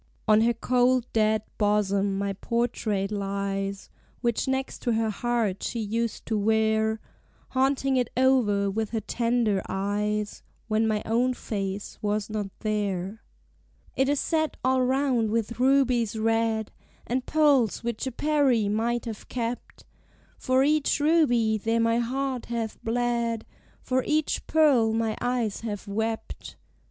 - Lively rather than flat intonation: No, average, 3.0 semitones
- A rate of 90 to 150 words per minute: Yes, average, 140 wpm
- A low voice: No, high, 230 Hz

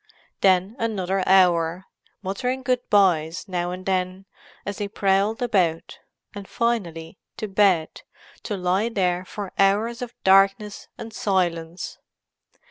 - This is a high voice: Yes, high, 195 Hz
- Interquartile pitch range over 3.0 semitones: No, narrow, 2.6 semitones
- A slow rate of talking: Yes, slow, 120 wpm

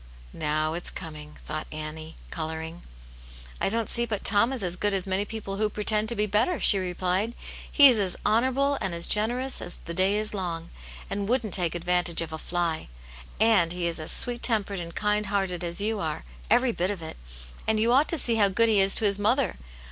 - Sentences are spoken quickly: Yes, fast, 215 wpm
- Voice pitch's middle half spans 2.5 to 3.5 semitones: No, average, 4.3 semitones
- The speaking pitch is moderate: No, high, 195 Hz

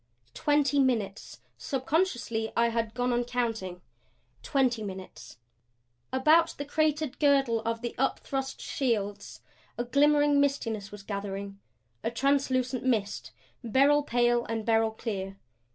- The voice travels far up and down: No, average, 4.0 semitones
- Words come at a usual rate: No, slow, 120 wpm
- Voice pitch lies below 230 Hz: No, high, 240 Hz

